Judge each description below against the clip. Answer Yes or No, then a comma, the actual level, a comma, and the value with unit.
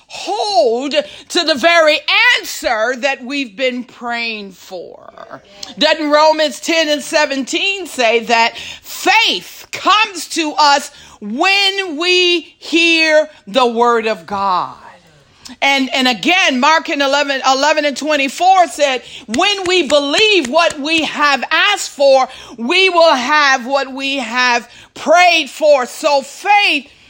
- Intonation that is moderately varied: Yes, average, 4.0 semitones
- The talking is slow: Yes, slow, 125 wpm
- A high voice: Yes, very high, 295 Hz